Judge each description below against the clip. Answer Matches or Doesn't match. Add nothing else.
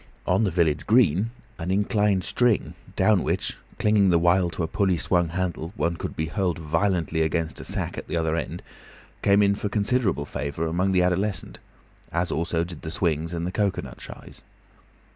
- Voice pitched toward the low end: Matches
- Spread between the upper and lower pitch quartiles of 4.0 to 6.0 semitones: Doesn't match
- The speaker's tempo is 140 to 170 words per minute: Doesn't match